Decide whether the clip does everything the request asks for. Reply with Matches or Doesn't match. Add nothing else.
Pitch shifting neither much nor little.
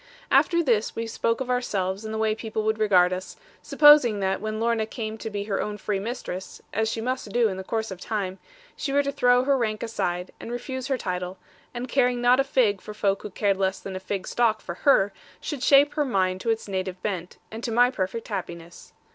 Matches